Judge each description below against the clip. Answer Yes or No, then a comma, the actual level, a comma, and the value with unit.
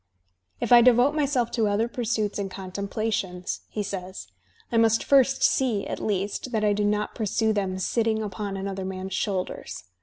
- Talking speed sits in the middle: Yes, average, 170 wpm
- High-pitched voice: Yes, high, 210 Hz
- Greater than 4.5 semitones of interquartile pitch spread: No, average, 2.9 semitones